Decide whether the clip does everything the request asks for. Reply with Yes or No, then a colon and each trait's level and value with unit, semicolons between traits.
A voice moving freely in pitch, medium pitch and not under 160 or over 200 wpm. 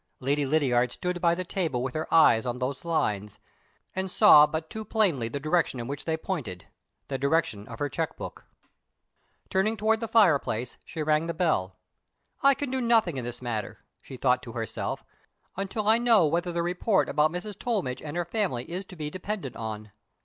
Yes: wide, 6.8 semitones; medium, 160 Hz; average, 195 wpm